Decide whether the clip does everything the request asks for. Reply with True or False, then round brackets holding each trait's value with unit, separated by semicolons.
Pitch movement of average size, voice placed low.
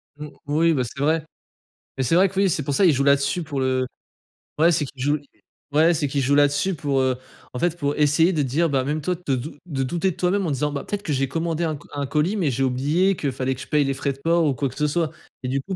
False (3.4 semitones; 150 Hz)